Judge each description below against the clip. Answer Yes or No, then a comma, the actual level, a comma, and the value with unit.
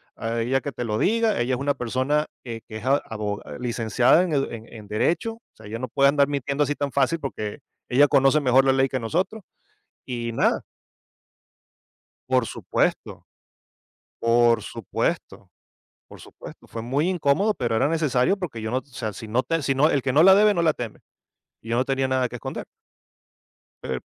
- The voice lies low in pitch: Yes, low, 130 Hz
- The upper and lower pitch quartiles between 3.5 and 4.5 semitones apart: Yes, average, 3.9 semitones